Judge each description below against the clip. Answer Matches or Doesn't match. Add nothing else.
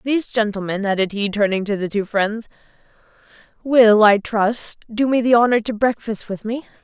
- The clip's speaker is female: Matches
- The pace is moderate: Matches